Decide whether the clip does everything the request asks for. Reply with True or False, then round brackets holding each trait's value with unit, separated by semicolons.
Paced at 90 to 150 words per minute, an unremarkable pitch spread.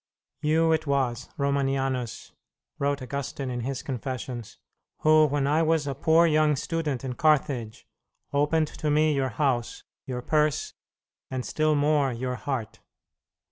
True (140 wpm; 3.0 semitones)